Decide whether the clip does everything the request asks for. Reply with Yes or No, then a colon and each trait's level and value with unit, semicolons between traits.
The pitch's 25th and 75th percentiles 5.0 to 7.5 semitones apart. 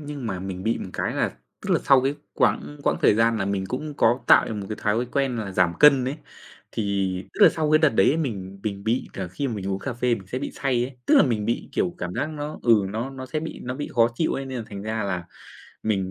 Yes: wide, 5.5 semitones